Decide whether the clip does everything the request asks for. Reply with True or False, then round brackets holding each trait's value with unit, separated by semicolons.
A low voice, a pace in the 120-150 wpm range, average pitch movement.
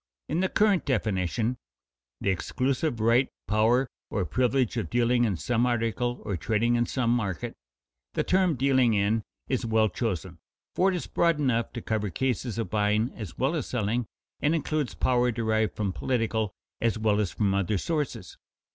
False (115 Hz; 170 wpm; 3.3 semitones)